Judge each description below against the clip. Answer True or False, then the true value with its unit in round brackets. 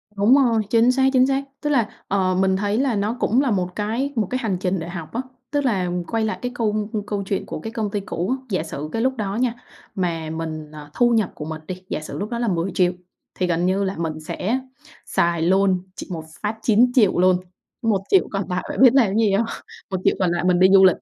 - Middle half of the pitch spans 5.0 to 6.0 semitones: False (4.3 semitones)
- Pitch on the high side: True (200 Hz)